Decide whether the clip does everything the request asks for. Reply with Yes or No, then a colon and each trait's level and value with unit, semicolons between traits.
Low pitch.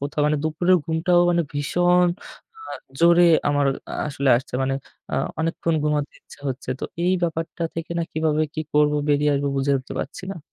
No: medium, 155 Hz